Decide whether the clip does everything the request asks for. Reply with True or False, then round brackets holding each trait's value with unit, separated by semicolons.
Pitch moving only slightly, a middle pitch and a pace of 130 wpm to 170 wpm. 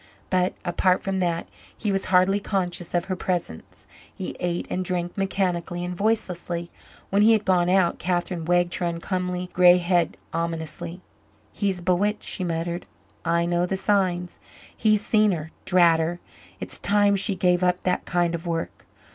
True (1.7 semitones; 180 Hz; 165 wpm)